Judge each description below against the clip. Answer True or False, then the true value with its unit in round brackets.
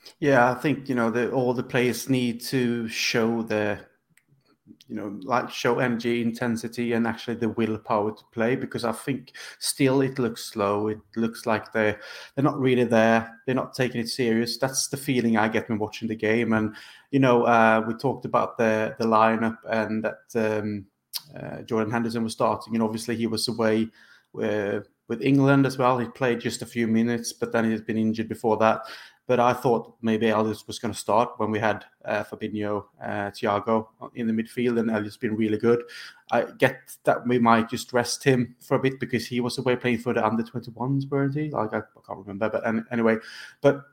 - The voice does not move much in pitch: True (2.0 semitones)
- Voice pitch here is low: True (115 Hz)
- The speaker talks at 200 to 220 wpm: True (205 wpm)